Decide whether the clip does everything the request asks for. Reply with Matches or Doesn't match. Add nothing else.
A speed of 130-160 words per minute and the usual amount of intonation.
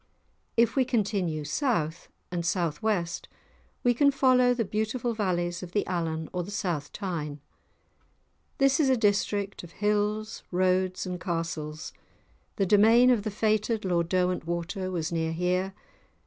Matches